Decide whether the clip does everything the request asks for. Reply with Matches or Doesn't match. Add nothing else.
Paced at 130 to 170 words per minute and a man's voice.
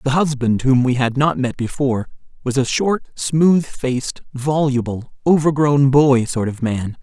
Matches